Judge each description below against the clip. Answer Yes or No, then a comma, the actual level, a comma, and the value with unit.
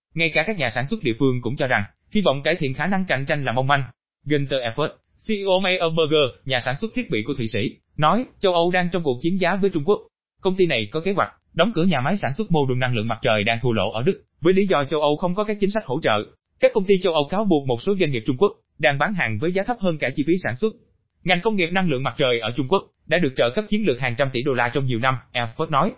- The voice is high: No, medium, 155 Hz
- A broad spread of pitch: Yes, wide, 6.8 semitones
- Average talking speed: No, fast, 305 wpm